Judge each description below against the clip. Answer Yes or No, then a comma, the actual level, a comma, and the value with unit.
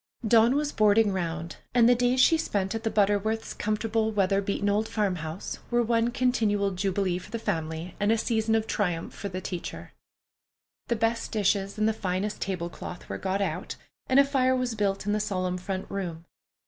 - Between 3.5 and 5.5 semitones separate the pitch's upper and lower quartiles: No, average, 3.1 semitones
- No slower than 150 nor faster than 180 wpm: No, average, 190 wpm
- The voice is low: No, high, 205 Hz